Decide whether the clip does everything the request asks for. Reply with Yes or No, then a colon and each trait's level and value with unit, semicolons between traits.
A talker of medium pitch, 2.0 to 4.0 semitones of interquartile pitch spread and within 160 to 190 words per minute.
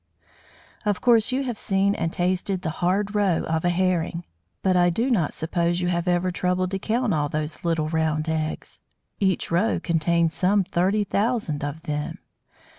Yes: medium, 180 Hz; average, 3.5 semitones; average, 175 wpm